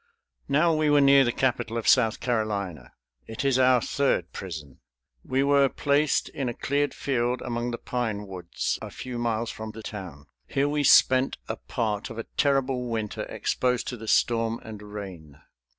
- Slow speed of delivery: No, average, 175 wpm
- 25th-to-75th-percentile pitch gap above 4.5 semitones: No, average, 4.0 semitones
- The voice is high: No, low, 120 Hz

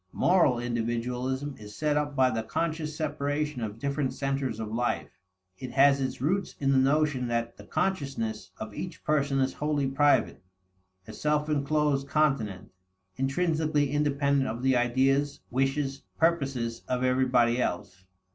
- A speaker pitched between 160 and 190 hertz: No, low, 135 Hz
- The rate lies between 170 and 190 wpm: No, average, 145 wpm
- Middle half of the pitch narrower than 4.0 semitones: Yes, average, 3.3 semitones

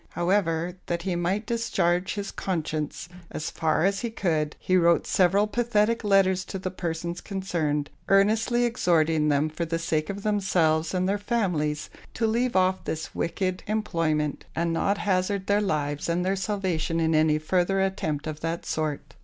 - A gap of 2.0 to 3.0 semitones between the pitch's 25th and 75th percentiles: No, average, 3.8 semitones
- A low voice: No, medium, 180 Hz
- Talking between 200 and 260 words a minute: No, average, 165 wpm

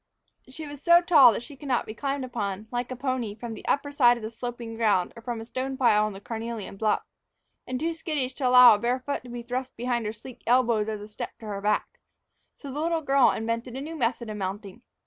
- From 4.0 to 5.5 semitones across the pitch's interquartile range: No, average, 3.2 semitones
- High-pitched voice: Yes, high, 240 Hz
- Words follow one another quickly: Yes, fast, 245 wpm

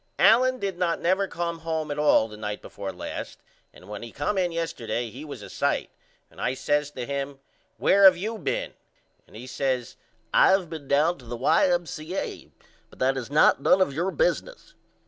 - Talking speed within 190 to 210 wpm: Yes, average, 195 wpm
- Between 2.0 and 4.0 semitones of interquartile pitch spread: No, wide, 5.6 semitones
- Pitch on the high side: No, medium, 155 Hz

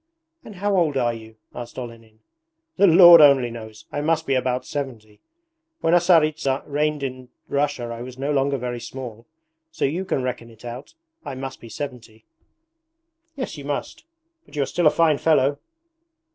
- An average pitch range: Yes, average, 4.1 semitones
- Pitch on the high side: No, low, 135 Hz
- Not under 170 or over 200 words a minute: Yes, average, 175 wpm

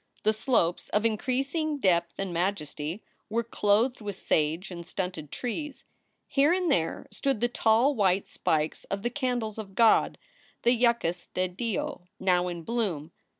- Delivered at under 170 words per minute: Yes, average, 150 wpm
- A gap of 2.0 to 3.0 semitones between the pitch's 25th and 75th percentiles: No, wide, 5.5 semitones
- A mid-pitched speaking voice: No, high, 210 Hz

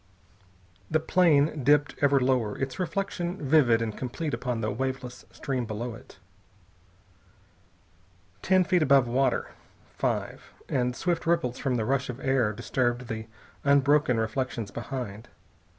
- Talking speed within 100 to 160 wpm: Yes, slow, 135 wpm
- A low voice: Yes, low, 130 Hz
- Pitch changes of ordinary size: Yes, average, 3.5 semitones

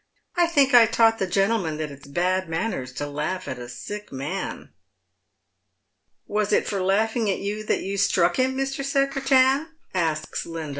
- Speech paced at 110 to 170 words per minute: No, average, 180 wpm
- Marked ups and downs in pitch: Yes, wide, 6.9 semitones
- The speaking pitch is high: Yes, high, 200 Hz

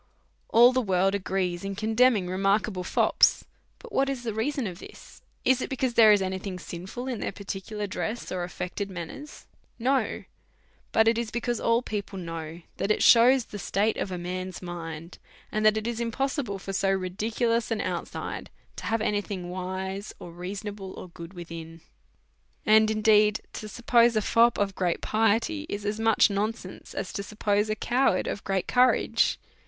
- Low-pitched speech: No, high, 205 Hz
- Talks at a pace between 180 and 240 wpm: Yes, average, 185 wpm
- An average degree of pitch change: Yes, average, 3.6 semitones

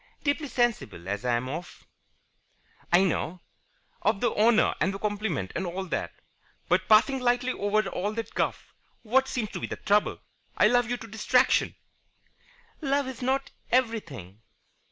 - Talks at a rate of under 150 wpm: No, average, 165 wpm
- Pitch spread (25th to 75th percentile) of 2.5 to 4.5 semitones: No, wide, 5.4 semitones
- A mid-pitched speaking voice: No, high, 215 Hz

